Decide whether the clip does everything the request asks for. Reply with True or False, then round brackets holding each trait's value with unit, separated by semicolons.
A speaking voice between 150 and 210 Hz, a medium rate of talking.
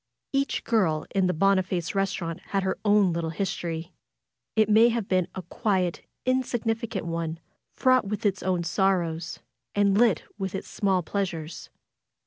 True (190 Hz; 145 wpm)